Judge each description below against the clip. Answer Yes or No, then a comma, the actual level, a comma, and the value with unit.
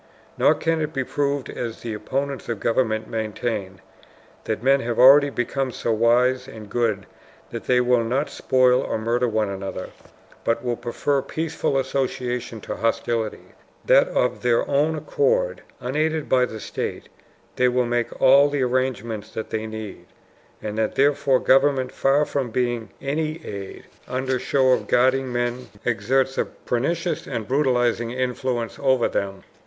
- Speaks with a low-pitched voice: Yes, low, 125 Hz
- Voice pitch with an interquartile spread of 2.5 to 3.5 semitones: Yes, average, 3.0 semitones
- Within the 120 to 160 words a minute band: Yes, average, 155 wpm